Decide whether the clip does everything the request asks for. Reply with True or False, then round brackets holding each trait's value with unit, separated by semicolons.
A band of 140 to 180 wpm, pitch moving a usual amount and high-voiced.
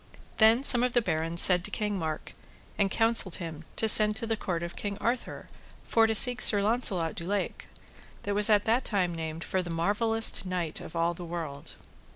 False (195 wpm; 4.8 semitones; 200 Hz)